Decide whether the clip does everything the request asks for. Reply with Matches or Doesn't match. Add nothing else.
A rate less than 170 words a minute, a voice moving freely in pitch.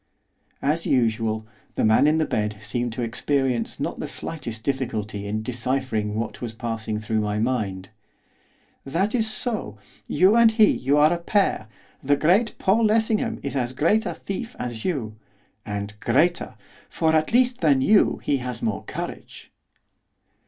Matches